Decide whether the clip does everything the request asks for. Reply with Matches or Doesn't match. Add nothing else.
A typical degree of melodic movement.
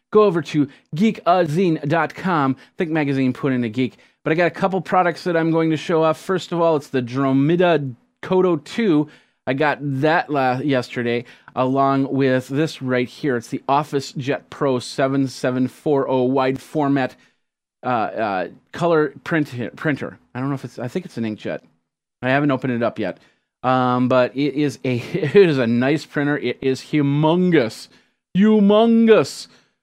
Matches